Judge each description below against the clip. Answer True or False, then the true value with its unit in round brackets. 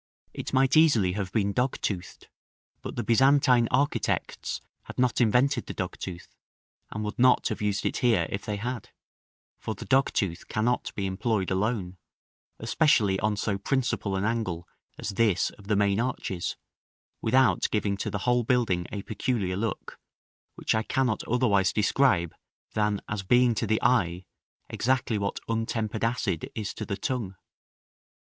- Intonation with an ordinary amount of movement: True (3.8 semitones)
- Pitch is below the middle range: True (110 Hz)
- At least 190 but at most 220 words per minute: False (155 wpm)